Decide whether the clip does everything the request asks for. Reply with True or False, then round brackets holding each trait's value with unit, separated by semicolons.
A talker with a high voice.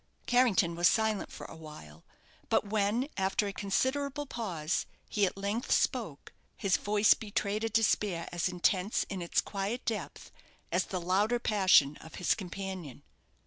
True (200 Hz)